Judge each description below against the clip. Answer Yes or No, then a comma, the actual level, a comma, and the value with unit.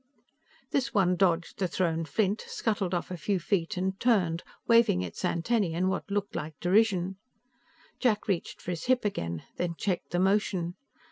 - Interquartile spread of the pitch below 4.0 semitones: Yes, average, 3.4 semitones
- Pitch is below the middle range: No, medium, 185 Hz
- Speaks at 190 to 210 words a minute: No, average, 165 wpm